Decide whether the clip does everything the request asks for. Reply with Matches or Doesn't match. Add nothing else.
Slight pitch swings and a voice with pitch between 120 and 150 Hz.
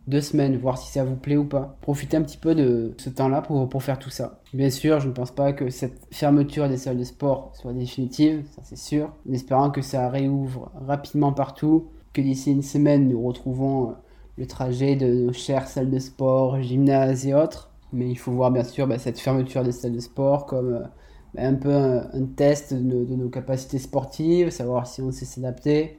Matches